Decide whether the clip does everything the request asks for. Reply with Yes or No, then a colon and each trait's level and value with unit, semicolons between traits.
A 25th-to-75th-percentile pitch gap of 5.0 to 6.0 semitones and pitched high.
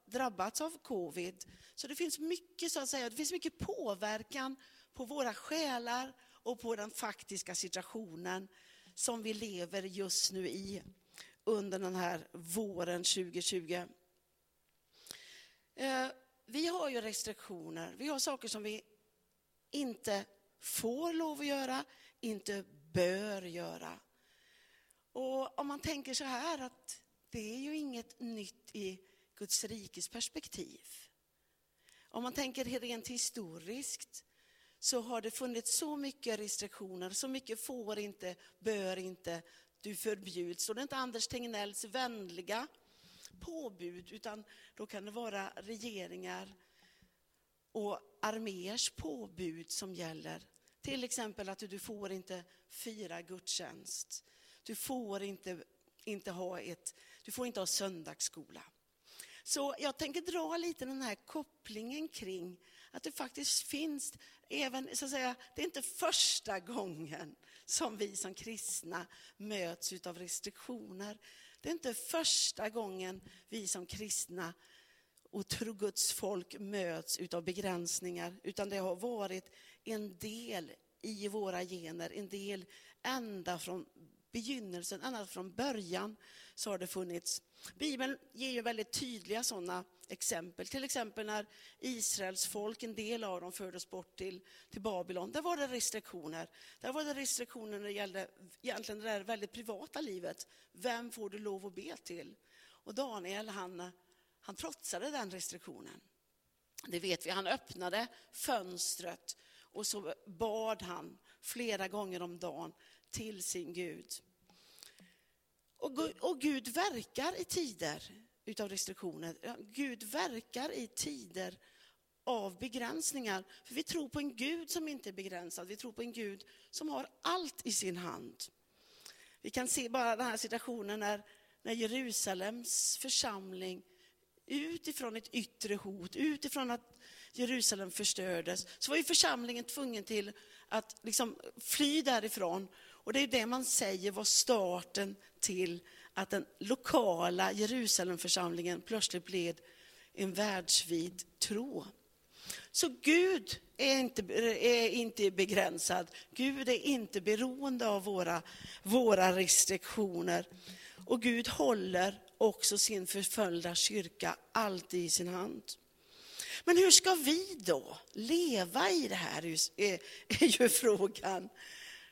Yes: average, 5.3 semitones; high, 215 Hz